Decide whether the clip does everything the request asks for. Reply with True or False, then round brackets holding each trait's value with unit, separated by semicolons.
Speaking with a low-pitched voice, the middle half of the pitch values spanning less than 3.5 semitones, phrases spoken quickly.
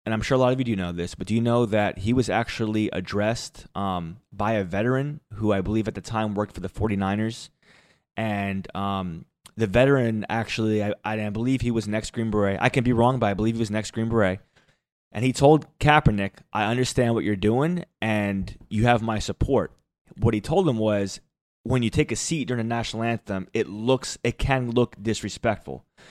True (110 Hz; 2.9 semitones; 215 wpm)